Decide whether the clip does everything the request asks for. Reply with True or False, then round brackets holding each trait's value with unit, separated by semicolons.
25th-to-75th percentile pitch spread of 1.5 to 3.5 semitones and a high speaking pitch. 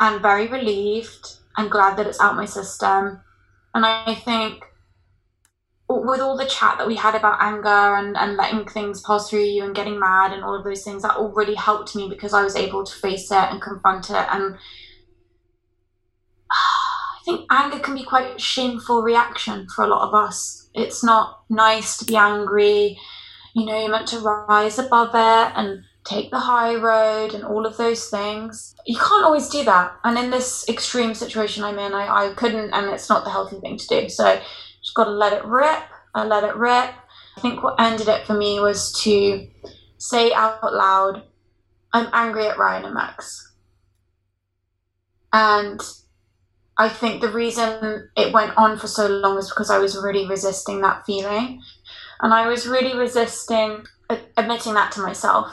True (2.7 semitones; 210 Hz)